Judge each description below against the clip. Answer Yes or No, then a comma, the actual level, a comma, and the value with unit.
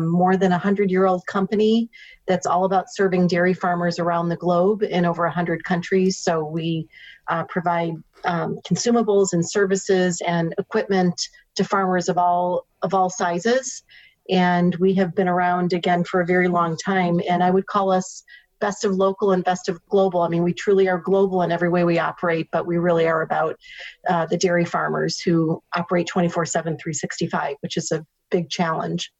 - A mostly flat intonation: Yes, narrow, 1.9 semitones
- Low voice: No, medium, 180 Hz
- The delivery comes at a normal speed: Yes, average, 185 wpm